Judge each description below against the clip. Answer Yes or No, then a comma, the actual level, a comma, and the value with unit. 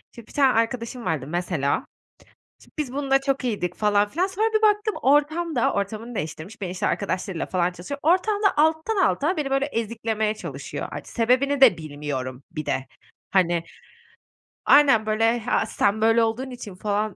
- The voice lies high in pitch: Yes, high, 225 Hz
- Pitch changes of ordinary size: No, wide, 6.7 semitones